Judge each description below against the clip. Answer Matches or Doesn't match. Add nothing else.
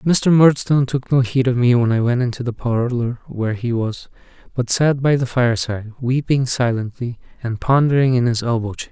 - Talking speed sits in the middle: Matches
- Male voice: Matches